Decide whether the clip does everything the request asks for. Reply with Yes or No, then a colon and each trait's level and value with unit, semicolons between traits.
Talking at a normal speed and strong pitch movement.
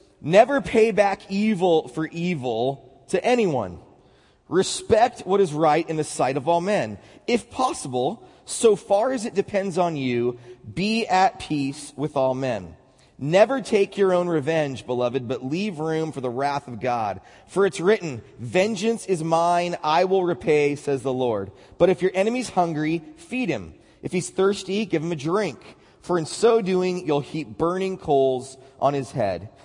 Yes: average, 170 wpm; wide, 6.2 semitones